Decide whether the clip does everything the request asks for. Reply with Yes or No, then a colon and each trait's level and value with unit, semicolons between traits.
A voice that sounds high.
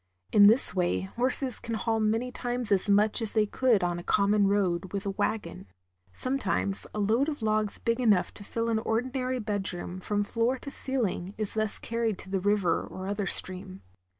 Yes: high, 210 Hz